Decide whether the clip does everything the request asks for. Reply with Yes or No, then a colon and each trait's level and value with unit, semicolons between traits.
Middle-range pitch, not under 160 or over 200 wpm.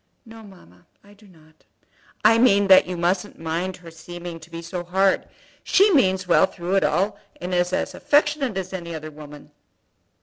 Yes: medium, 180 Hz; average, 180 wpm